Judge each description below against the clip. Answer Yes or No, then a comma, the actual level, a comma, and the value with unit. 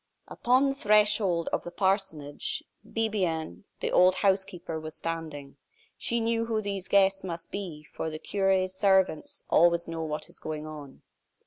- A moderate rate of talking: Yes, average, 150 wpm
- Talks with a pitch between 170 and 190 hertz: Yes, medium, 185 Hz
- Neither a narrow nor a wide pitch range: Yes, average, 4.0 semitones